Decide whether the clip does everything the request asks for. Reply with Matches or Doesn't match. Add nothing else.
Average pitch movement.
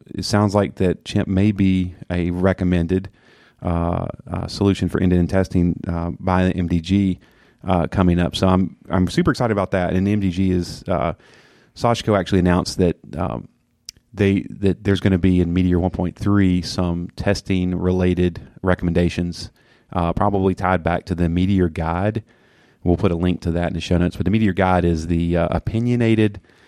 Doesn't match